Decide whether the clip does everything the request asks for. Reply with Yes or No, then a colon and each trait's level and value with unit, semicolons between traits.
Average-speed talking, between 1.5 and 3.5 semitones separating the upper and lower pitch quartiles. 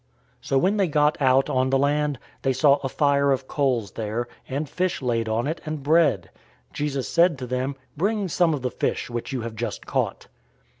No: fast, 210 wpm; average, 2.9 semitones